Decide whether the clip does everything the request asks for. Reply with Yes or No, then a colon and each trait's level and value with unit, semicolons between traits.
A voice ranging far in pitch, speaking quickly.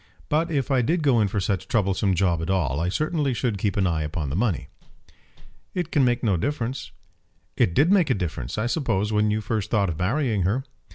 Yes: wide, 6.3 semitones; fast, 225 wpm